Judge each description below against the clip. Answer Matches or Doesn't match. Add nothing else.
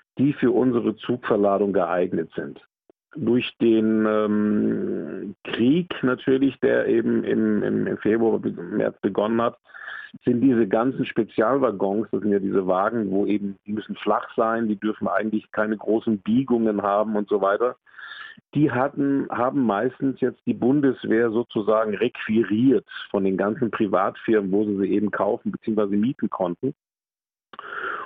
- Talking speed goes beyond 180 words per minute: Doesn't match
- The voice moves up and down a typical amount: Matches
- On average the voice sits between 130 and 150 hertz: Doesn't match